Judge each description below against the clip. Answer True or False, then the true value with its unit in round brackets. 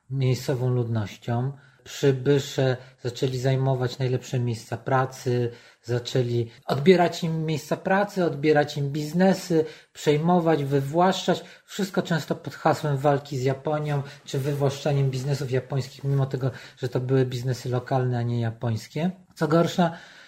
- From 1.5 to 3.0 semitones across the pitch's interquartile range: False (3.6 semitones)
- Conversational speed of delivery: True (120 wpm)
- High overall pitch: False (140 Hz)